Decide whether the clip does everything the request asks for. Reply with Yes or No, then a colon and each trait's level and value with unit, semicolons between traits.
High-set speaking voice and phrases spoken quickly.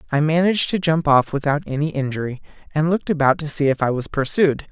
No: medium, 150 Hz; fast, 215 wpm